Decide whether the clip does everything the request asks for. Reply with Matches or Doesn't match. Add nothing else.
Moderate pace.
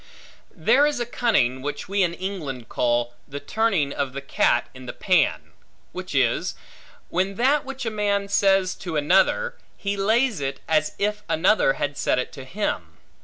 Matches